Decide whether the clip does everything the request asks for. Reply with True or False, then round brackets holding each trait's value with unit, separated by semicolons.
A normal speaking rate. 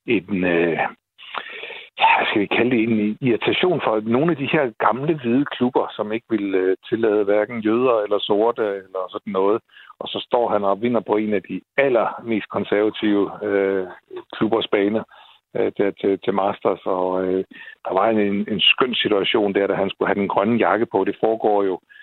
True (190 wpm)